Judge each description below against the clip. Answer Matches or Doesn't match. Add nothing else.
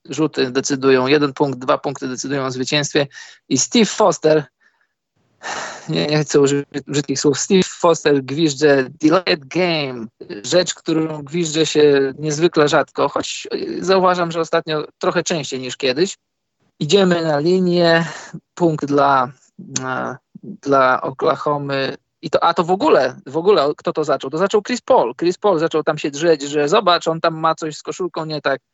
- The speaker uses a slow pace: Doesn't match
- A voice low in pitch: Doesn't match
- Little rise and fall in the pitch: Doesn't match